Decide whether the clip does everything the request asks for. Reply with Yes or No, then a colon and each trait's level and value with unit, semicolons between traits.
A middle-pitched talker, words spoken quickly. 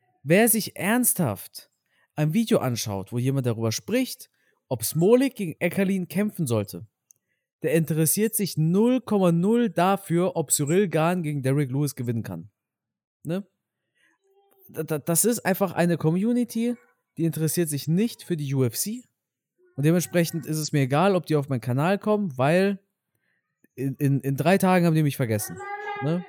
No: medium, 170 Hz; average, 150 wpm